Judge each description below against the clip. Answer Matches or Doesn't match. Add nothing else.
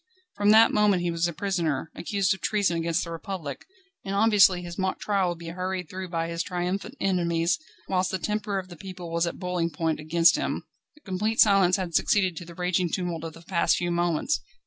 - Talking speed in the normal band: Doesn't match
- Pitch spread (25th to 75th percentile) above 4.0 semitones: Doesn't match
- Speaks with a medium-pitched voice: Matches